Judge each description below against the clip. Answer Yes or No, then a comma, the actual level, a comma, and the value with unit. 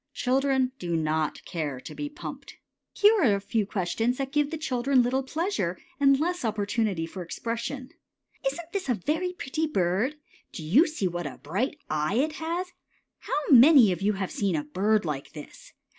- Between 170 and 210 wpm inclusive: Yes, average, 180 wpm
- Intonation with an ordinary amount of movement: No, wide, 8.2 semitones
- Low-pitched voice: No, high, 235 Hz